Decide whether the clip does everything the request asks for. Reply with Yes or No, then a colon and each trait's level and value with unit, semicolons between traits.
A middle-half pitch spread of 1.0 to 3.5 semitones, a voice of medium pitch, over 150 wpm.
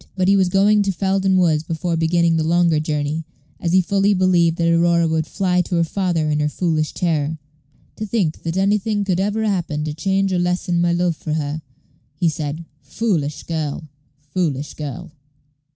Yes: average, 3.1 semitones; medium, 170 Hz; average, 185 wpm